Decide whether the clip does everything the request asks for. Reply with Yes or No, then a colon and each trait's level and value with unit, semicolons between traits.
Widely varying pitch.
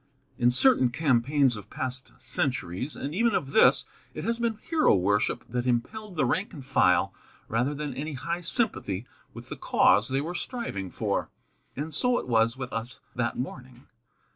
Yes: wide, 6.0 semitones